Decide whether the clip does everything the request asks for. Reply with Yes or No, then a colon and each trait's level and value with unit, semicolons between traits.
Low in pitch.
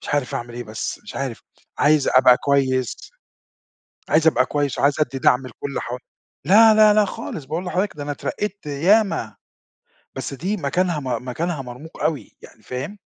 No: medium, 145 Hz